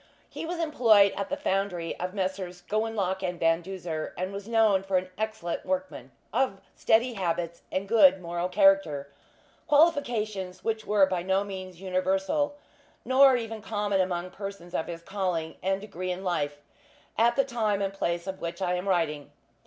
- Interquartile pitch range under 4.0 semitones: Yes, average, 3.3 semitones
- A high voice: Yes, high, 195 Hz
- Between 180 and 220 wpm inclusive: No, average, 170 wpm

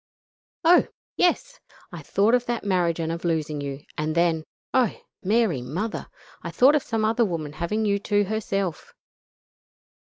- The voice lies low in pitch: No, high, 195 Hz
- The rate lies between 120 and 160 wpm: Yes, average, 155 wpm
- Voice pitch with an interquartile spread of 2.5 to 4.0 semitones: No, wide, 5.6 semitones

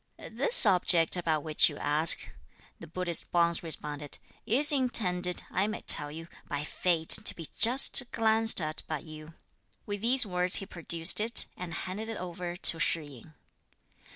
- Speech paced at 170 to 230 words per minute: No, average, 160 wpm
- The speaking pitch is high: No, medium, 175 Hz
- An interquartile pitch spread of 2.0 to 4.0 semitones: No, average, 4.8 semitones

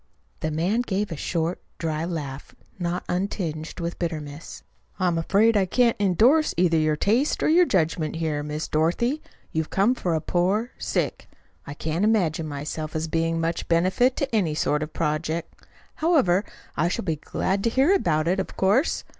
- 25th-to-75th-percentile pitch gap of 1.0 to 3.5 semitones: No, average, 4.6 semitones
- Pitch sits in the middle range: Yes, medium, 170 Hz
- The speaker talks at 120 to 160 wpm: No, average, 170 wpm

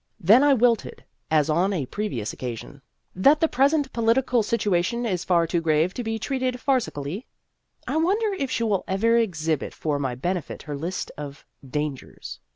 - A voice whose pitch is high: Yes, high, 195 Hz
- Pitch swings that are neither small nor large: No, wide, 8.0 semitones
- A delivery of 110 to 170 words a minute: No, average, 190 wpm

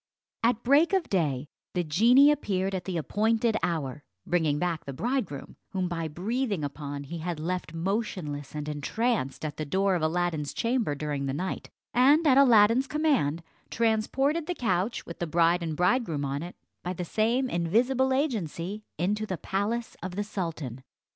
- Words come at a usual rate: Yes, average, 165 wpm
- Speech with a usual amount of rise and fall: No, wide, 6.8 semitones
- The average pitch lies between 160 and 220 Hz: Yes, medium, 185 Hz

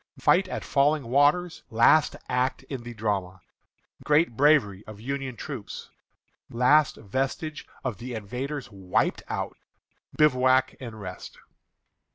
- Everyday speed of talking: No, slow, 120 wpm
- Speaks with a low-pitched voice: Yes, low, 130 Hz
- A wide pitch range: No, average, 4.6 semitones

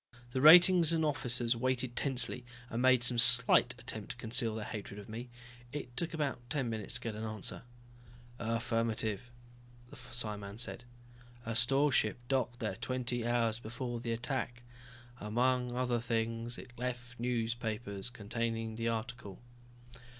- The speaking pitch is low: Yes, low, 120 Hz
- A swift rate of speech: No, average, 145 wpm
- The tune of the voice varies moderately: No, narrow, 1.8 semitones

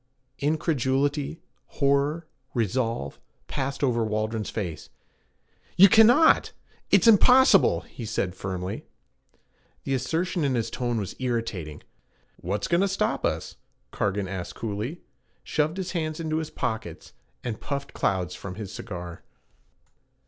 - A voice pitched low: Yes, low, 125 Hz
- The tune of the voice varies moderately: No, wide, 7.6 semitones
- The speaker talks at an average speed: No, slow, 120 wpm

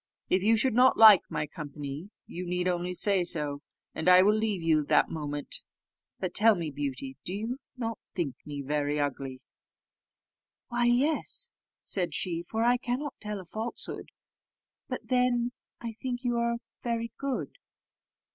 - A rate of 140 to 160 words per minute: Yes, average, 155 wpm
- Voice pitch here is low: No, high, 190 Hz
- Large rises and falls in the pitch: Yes, wide, 7.6 semitones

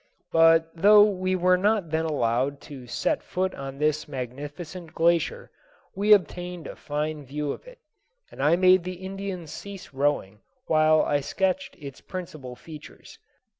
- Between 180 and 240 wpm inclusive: No, average, 150 wpm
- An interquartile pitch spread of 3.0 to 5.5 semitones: Yes, average, 4.2 semitones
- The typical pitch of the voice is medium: Yes, medium, 165 Hz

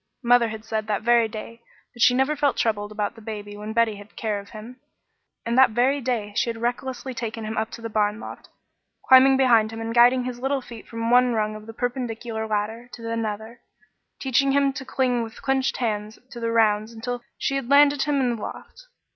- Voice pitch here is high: Yes, high, 230 Hz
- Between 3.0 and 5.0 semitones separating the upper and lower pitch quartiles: No, narrow, 2.6 semitones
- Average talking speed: No, fast, 215 wpm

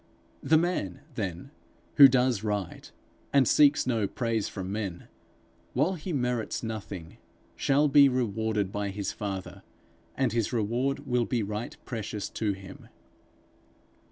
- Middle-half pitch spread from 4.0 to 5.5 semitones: Yes, average, 4.5 semitones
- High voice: No, low, 110 Hz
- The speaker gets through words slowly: Yes, slow, 130 wpm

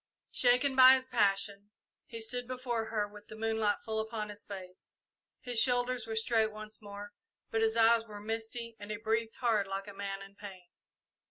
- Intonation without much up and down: Yes, narrow, 2.1 semitones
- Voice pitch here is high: Yes, high, 220 Hz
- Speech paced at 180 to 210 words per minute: Yes, average, 185 wpm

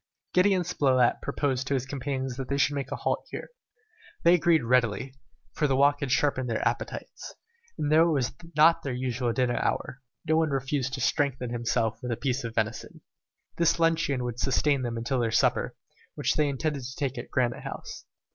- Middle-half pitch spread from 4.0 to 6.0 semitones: No, average, 2.9 semitones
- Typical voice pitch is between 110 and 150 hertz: Yes, low, 135 Hz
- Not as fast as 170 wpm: No, average, 195 wpm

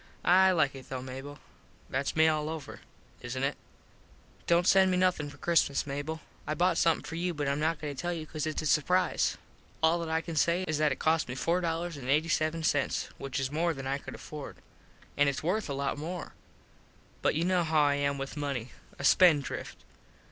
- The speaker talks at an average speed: No, fast, 215 wpm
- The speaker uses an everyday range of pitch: Yes, average, 3.1 semitones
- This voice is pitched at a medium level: Yes, medium, 155 Hz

